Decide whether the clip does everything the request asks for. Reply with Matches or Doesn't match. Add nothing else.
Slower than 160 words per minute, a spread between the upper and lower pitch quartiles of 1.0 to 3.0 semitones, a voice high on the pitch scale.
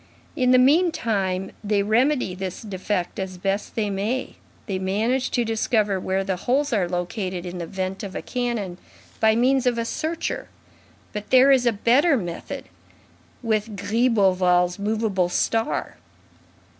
Doesn't match